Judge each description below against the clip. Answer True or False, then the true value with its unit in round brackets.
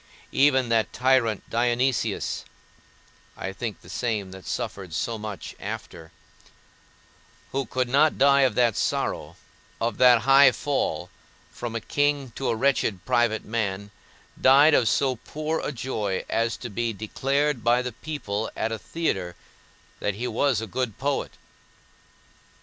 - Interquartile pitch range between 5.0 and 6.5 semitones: False (3.9 semitones)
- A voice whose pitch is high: False (120 Hz)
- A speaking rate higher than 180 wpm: False (145 wpm)